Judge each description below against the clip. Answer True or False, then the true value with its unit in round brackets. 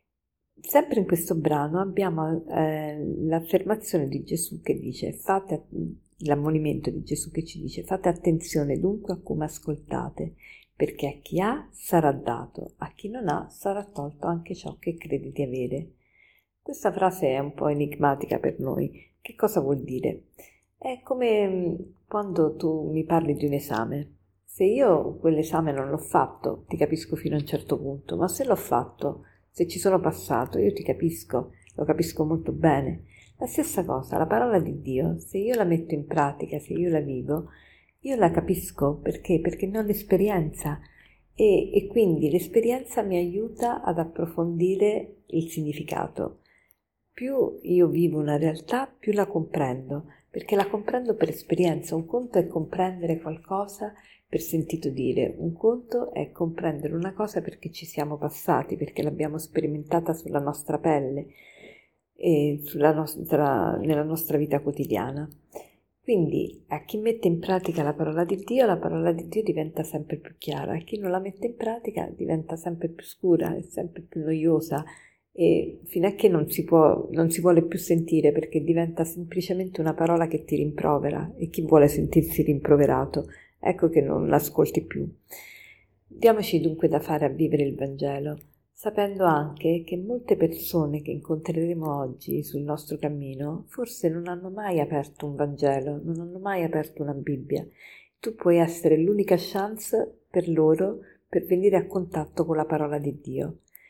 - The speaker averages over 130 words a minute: True (160 wpm)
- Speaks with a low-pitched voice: False (165 Hz)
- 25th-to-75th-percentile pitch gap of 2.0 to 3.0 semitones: False (3.7 semitones)